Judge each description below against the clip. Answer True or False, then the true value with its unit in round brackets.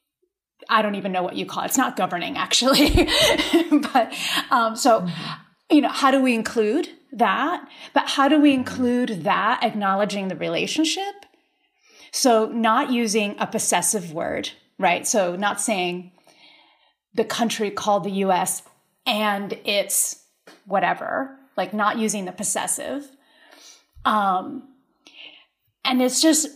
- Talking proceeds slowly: True (130 wpm)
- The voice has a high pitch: True (245 Hz)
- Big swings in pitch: True (6.5 semitones)